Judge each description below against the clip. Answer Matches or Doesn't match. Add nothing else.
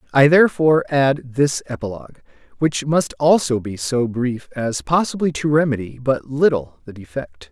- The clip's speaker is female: Doesn't match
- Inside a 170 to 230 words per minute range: Doesn't match